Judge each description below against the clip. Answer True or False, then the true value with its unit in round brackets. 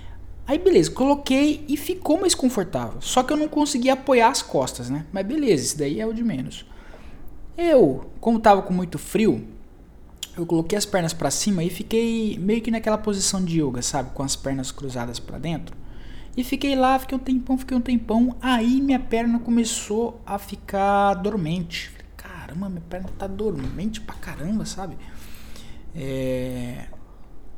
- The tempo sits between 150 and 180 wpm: True (170 wpm)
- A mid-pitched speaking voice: False (200 Hz)